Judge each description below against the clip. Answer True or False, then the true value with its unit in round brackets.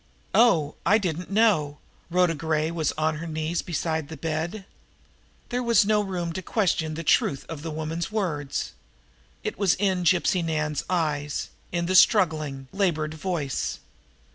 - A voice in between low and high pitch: True (165 Hz)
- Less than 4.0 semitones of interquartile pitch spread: True (3.2 semitones)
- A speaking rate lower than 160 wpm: True (150 wpm)